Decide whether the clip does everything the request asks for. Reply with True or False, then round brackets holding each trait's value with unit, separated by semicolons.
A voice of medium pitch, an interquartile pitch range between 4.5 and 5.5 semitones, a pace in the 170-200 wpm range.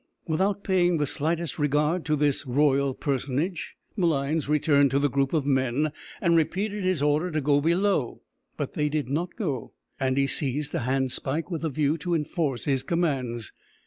False (150 Hz; 3.5 semitones; 175 wpm)